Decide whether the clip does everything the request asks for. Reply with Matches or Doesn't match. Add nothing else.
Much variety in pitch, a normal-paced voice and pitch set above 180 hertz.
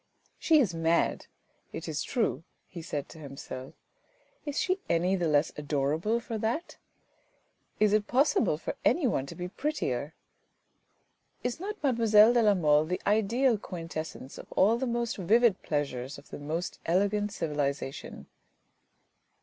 Matches